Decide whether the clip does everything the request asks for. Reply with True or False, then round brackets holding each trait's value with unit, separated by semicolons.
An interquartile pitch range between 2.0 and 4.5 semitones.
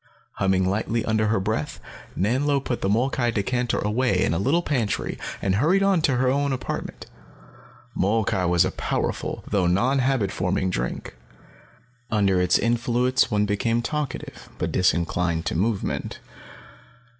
False (5.1 semitones)